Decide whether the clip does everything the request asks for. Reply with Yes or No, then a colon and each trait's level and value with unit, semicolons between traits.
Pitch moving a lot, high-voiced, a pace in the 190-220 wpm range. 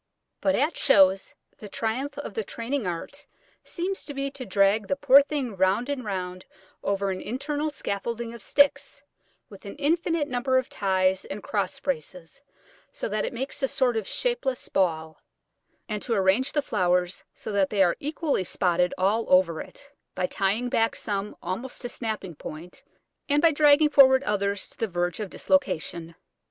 No: wide, 6.6 semitones; high, 215 Hz; average, 170 wpm